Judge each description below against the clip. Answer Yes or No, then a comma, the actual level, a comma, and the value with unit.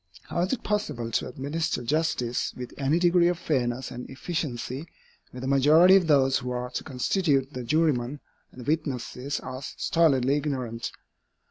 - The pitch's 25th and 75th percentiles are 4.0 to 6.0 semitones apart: Yes, average, 4.3 semitones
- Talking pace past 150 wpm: Yes, average, 160 wpm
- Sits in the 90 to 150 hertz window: Yes, medium, 140 Hz